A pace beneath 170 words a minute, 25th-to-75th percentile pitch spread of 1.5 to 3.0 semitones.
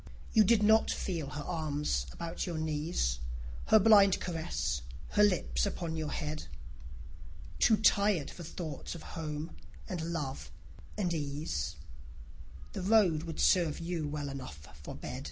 No: average, 140 wpm; average, 3.7 semitones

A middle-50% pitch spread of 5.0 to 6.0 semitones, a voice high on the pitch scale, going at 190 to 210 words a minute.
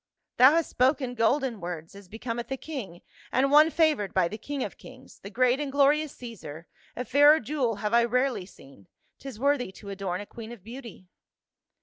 Yes: wide, 5.4 semitones; high, 245 Hz; average, 200 wpm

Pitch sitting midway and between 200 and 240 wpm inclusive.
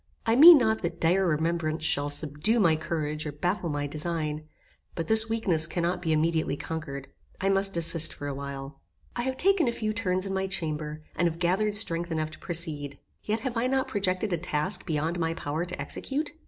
Yes: medium, 170 Hz; fast, 205 wpm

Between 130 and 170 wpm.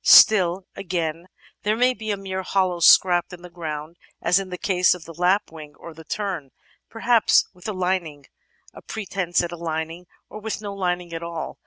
No: average, 200 wpm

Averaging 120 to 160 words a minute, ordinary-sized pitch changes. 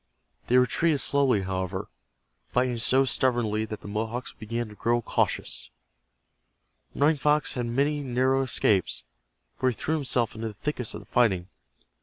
Yes: average, 150 wpm; average, 3.7 semitones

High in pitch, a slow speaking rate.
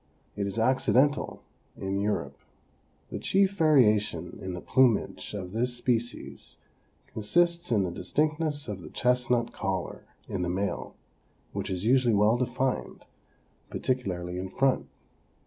No: low, 115 Hz; slow, 130 wpm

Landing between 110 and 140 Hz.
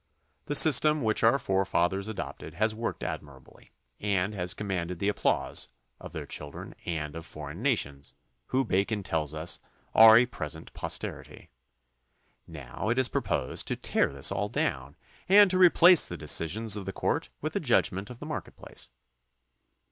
No: very low, 95 Hz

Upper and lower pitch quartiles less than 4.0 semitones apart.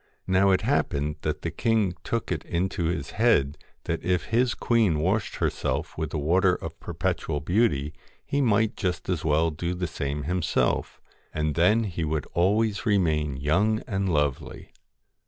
No: average, 5.3 semitones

